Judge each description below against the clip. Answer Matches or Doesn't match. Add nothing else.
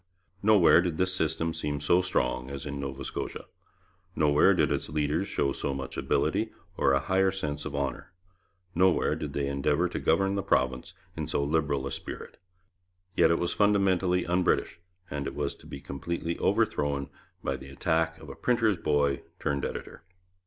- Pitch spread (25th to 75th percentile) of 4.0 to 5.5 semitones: Matches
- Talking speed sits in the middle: Matches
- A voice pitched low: Matches